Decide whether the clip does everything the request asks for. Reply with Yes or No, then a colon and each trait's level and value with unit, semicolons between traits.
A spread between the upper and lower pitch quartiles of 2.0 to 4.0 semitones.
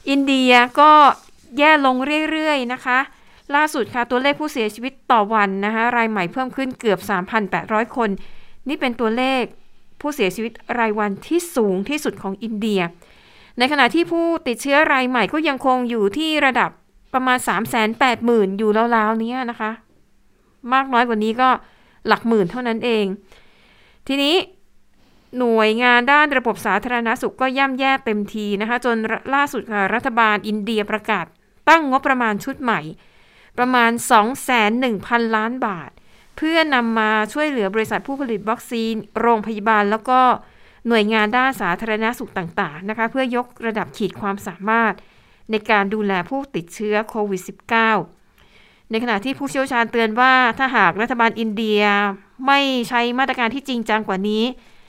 Yes: average, 3.4 semitones